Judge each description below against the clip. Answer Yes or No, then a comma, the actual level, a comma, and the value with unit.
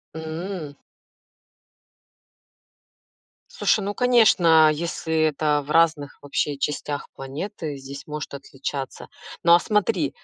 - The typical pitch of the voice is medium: Yes, medium, 155 Hz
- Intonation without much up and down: No, average, 3.1 semitones